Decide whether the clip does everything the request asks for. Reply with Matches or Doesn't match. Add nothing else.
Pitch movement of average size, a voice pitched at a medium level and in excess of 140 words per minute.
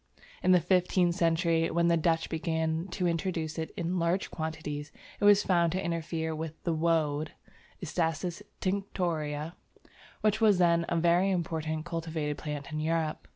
Doesn't match